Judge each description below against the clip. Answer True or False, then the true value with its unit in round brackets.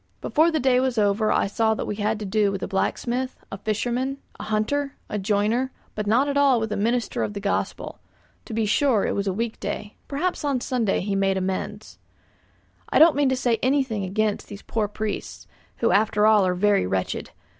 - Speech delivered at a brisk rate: True (210 wpm)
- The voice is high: True (215 Hz)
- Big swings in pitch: False (3.9 semitones)